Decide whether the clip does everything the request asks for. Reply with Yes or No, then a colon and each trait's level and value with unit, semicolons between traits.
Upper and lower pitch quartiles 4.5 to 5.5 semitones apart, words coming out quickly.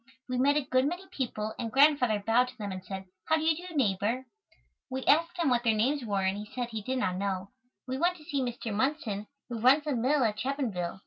Yes: average, 5.1 semitones; fast, 240 wpm